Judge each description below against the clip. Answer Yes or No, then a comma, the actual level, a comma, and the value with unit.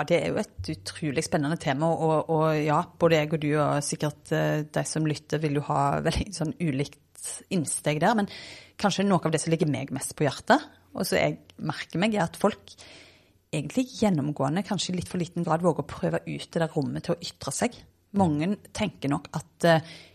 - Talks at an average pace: No, fast, 215 wpm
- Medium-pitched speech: Yes, medium, 160 Hz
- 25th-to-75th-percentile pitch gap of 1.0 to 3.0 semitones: Yes, average, 2.7 semitones